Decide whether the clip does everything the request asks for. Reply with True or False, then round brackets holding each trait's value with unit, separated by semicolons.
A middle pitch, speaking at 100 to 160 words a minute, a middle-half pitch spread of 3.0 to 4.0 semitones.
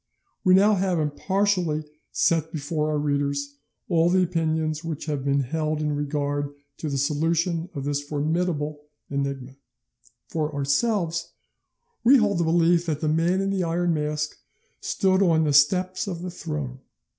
True (160 Hz; 155 wpm; 3.3 semitones)